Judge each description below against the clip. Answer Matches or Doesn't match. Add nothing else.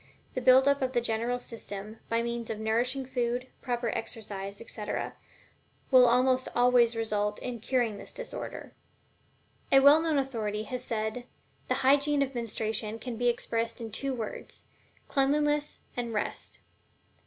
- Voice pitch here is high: Matches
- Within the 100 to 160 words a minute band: Matches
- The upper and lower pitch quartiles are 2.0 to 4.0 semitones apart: Matches